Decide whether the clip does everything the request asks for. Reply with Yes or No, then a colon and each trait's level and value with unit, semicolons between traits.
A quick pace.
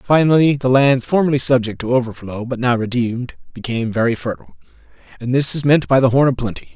No: average, 195 wpm